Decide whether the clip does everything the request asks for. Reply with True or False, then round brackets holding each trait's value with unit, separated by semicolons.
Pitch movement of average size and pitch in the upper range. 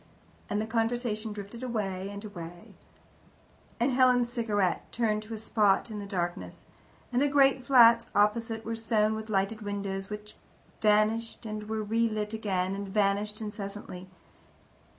False (2.1 semitones; 215 Hz)